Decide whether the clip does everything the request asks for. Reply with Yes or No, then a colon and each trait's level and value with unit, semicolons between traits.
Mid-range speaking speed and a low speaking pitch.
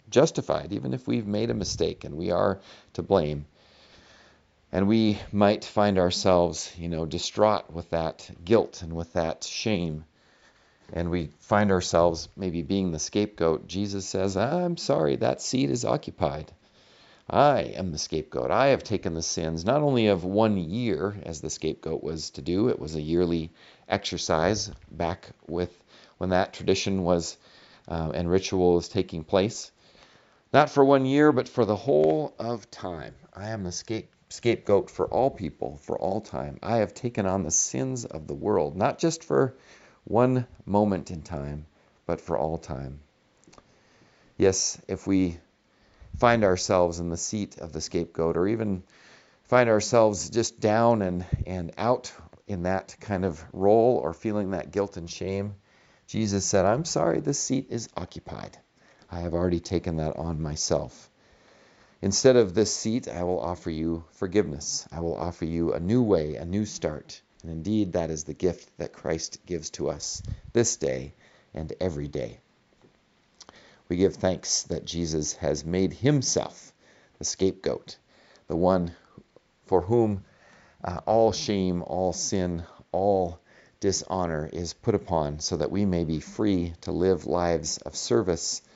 Yes: average, 160 wpm; very low, 90 Hz